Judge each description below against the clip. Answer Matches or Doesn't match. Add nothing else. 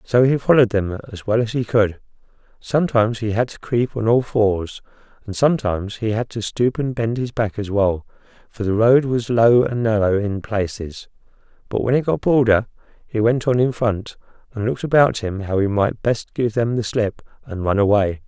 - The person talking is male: Matches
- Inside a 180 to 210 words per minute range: Matches